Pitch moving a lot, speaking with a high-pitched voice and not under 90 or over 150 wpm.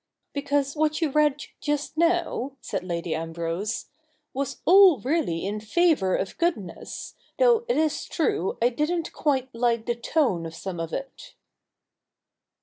Yes: wide, 8.2 semitones; very high, 275 Hz; average, 145 wpm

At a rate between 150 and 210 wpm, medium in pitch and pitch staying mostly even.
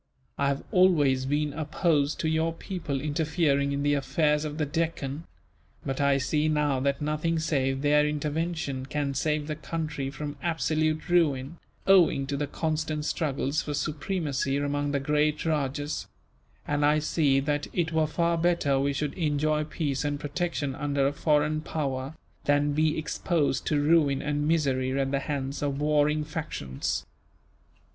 Yes: average, 155 wpm; medium, 150 Hz; narrow, 2.0 semitones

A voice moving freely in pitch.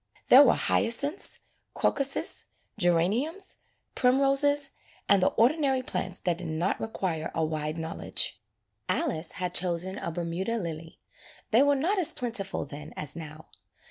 Yes: wide, 8.6 semitones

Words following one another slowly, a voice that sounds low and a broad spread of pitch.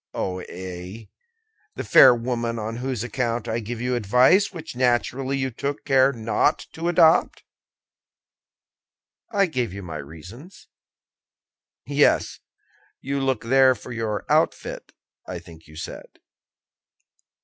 No: slow, 125 wpm; low, 120 Hz; average, 4.0 semitones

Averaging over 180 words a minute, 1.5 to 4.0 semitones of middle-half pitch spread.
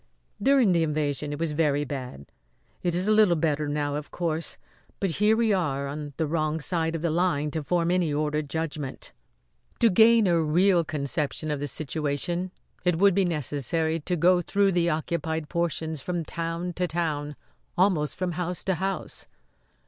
No: average, 175 wpm; average, 3.1 semitones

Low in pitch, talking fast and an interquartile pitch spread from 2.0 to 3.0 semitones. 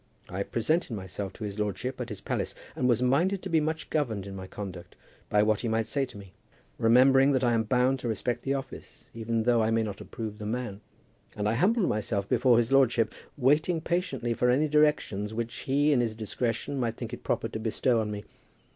No: low, 120 Hz; fast, 215 wpm; average, 3.9 semitones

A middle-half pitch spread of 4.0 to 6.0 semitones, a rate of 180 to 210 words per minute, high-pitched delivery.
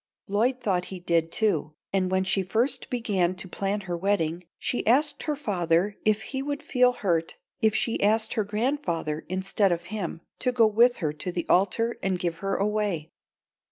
Yes: average, 4.5 semitones; average, 185 wpm; high, 200 Hz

